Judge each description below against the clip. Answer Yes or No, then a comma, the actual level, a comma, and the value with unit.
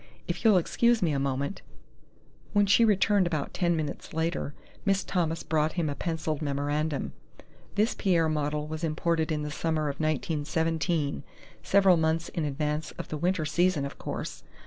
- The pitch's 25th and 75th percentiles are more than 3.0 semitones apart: No, average, 2.7 semitones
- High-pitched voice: No, medium, 160 Hz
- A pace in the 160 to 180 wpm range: Yes, average, 170 wpm